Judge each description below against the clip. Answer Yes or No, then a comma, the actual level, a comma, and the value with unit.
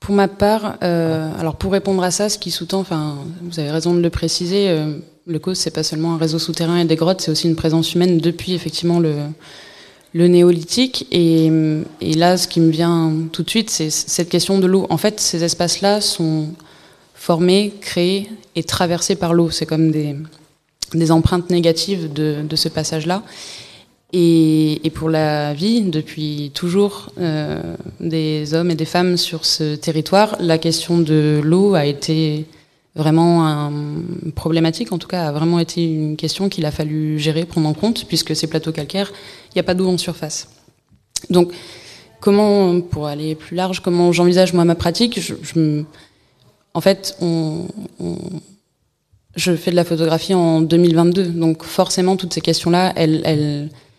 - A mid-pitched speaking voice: Yes, medium, 165 Hz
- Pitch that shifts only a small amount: Yes, narrow, 2.3 semitones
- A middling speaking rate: Yes, average, 175 wpm